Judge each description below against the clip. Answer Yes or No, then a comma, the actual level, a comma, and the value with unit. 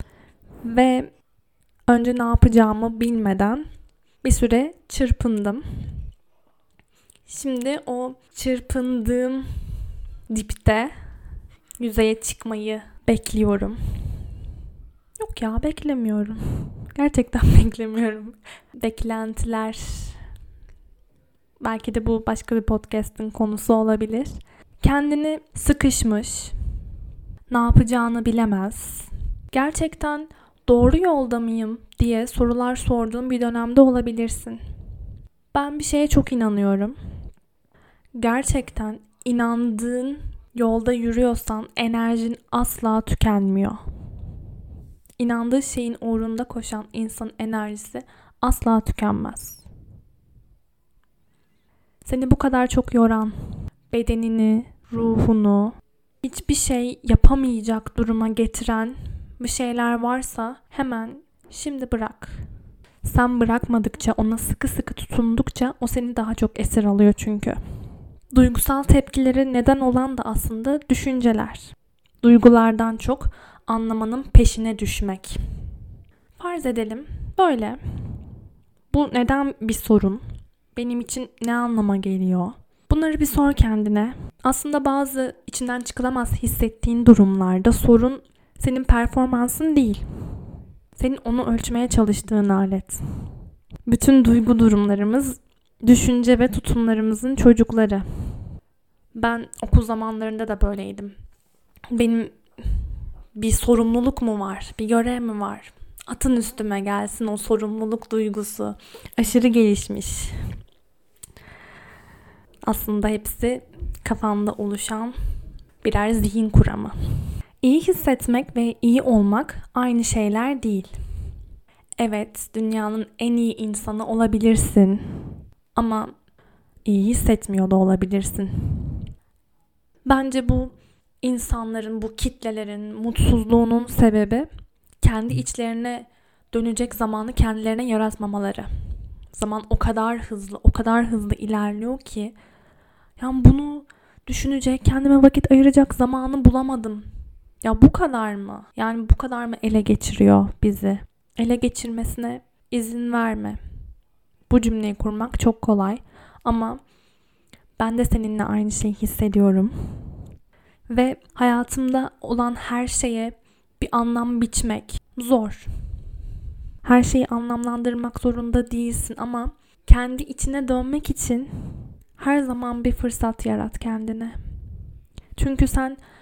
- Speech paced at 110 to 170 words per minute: No, slow, 95 wpm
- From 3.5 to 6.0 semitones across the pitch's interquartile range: No, narrow, 2.6 semitones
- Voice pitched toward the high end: Yes, high, 230 Hz